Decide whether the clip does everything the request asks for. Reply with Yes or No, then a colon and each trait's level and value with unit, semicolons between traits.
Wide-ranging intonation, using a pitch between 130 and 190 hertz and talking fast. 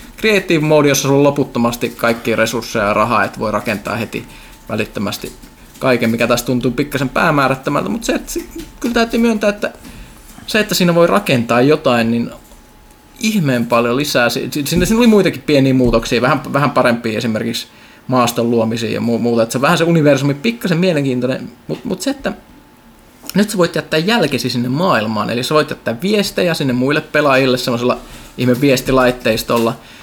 Yes: wide, 6.2 semitones; low, 135 Hz; fast, 165 wpm